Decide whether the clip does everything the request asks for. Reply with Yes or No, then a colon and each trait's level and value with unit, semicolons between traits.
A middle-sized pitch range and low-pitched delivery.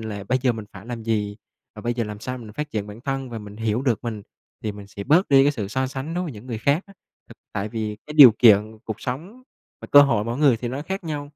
Yes: average, 4.8 semitones; low, 120 Hz